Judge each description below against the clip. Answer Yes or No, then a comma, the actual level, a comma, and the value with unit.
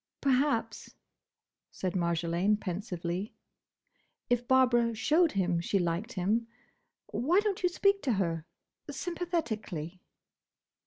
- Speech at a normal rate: No, slow, 95 wpm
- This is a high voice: Yes, high, 220 Hz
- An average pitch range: No, wide, 7.4 semitones